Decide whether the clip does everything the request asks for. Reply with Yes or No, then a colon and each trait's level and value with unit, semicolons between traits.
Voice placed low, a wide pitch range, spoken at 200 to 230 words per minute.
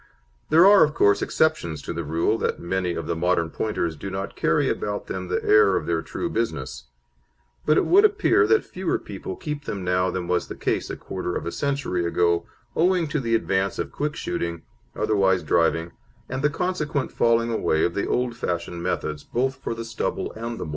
Yes: low, 100 Hz; wide, 8.0 semitones; fast, 205 wpm